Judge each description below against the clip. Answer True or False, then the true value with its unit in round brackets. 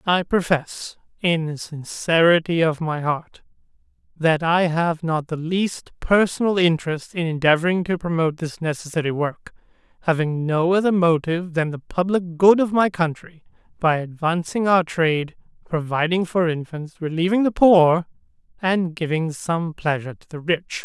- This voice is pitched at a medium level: True (165 Hz)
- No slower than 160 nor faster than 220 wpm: False (145 wpm)